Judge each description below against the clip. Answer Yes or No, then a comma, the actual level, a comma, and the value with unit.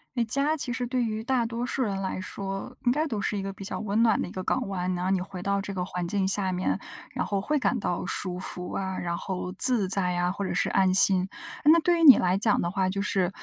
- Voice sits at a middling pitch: No, high, 195 Hz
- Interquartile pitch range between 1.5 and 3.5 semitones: No, average, 4.1 semitones